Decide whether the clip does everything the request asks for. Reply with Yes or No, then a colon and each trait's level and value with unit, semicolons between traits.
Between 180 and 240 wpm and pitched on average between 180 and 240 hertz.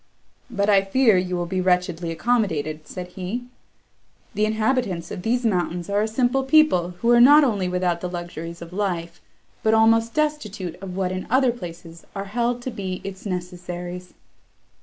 No: average, 170 wpm; high, 190 Hz